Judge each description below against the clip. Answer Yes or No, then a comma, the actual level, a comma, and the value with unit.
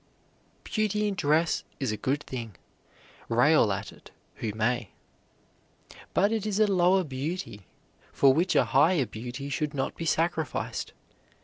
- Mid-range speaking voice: Yes, medium, 150 Hz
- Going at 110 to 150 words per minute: Yes, average, 140 wpm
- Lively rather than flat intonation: Yes, wide, 6.7 semitones